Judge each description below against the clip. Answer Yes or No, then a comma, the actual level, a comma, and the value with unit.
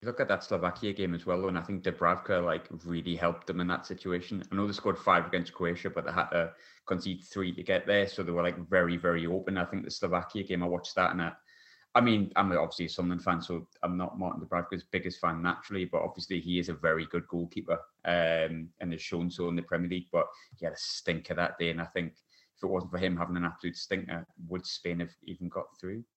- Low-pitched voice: Yes, very low, 90 Hz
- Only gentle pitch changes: Yes, narrow, 1.5 semitones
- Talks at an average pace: No, fast, 250 wpm